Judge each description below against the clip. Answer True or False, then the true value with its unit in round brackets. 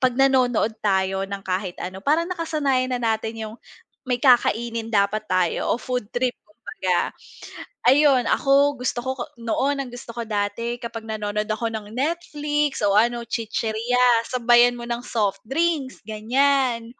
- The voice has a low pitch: False (235 Hz)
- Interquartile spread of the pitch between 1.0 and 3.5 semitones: True (3.2 semitones)